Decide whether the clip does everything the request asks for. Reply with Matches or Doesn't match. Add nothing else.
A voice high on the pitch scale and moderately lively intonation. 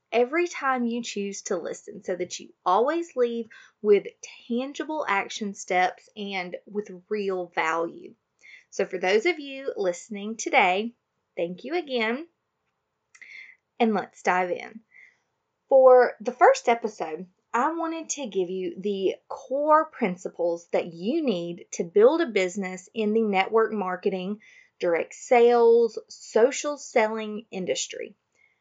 Doesn't match